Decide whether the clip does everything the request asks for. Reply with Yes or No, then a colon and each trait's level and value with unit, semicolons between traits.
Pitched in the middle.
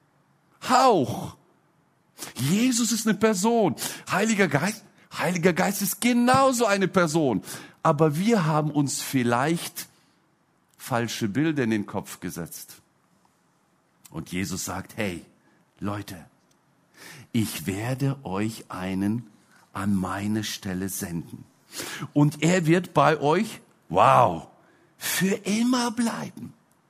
Yes: medium, 155 Hz